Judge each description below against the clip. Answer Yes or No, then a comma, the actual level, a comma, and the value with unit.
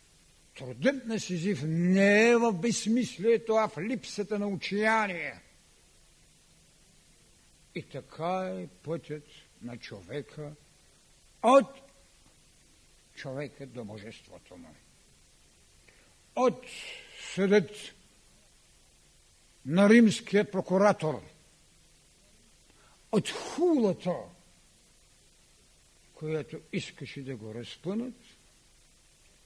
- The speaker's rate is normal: No, slow, 70 wpm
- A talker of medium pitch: Yes, medium, 170 Hz